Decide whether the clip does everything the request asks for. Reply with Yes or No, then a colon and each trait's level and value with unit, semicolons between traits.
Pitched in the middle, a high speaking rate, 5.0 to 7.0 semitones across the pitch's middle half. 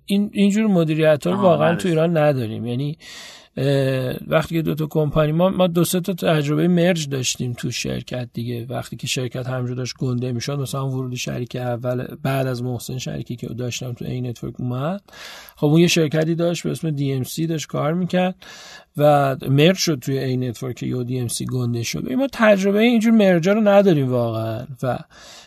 Yes: medium, 145 Hz; fast, 180 wpm; wide, 5.6 semitones